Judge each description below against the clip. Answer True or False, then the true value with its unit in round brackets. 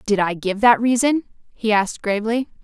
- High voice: True (220 Hz)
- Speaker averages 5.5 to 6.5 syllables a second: True (5.6 syllables/s)